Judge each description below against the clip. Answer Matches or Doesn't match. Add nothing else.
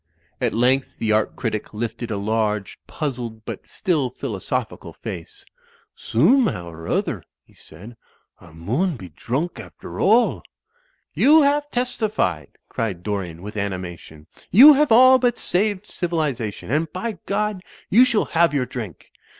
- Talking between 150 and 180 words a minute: Doesn't match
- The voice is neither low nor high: Doesn't match